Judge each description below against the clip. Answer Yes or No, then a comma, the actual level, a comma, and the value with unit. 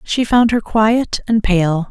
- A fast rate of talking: No, average, 190 wpm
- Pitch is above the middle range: Yes, high, 215 Hz